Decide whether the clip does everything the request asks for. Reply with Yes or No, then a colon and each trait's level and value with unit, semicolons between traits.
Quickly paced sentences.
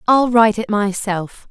No: average, 160 wpm